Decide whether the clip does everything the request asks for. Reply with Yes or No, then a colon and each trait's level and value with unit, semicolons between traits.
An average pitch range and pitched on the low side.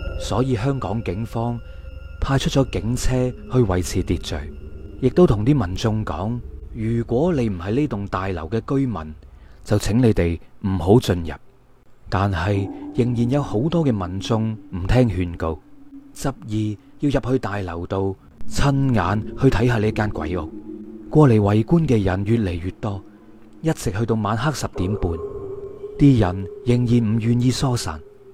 Yes: average, 5.0 semitones; low, 110 Hz